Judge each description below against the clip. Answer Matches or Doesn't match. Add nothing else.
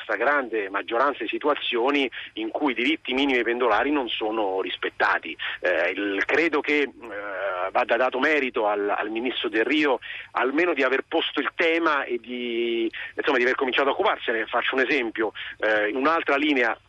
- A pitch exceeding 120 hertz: Matches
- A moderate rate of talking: Doesn't match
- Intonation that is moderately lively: Doesn't match